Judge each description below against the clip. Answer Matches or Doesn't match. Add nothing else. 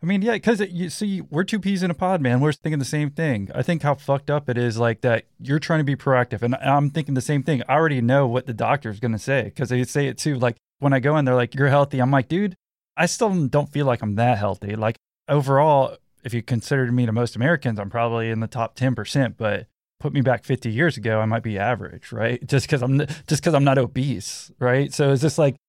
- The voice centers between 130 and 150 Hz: Matches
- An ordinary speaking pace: Doesn't match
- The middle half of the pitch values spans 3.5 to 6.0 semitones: Matches